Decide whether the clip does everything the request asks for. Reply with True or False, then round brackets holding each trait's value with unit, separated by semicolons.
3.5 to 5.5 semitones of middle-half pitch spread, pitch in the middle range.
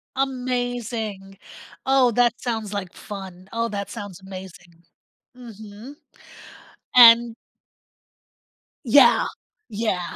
False (3.9 semitones; 220 Hz)